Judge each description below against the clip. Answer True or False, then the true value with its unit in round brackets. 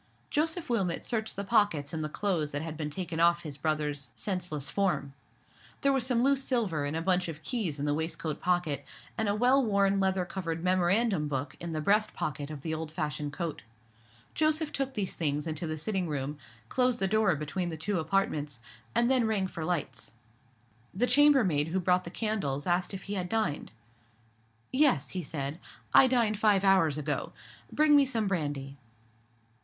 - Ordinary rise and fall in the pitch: False (6.0 semitones)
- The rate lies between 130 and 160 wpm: False (185 wpm)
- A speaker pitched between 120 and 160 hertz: False (180 Hz)